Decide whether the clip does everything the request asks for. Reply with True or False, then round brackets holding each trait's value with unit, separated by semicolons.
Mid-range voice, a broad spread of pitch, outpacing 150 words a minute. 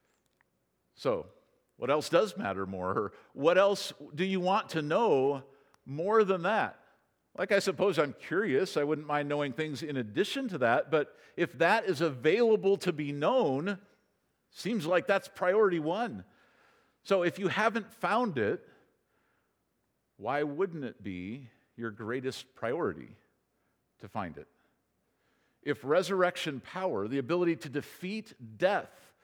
False (170 Hz; 5.9 semitones; 140 wpm)